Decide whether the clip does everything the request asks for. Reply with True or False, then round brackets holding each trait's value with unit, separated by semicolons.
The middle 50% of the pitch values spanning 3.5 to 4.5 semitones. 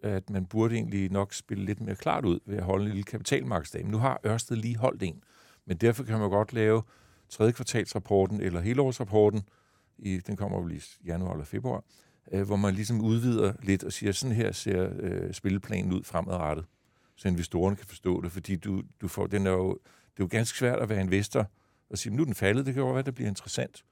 False (3.0 semitones)